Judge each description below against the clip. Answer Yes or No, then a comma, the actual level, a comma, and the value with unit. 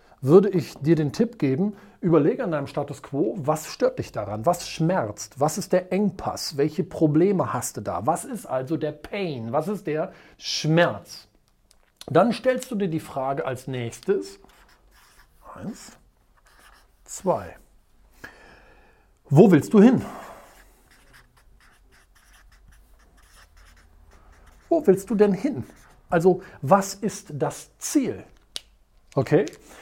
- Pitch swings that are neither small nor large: No, wide, 6.8 semitones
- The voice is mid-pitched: Yes, medium, 155 Hz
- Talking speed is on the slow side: Yes, slow, 120 wpm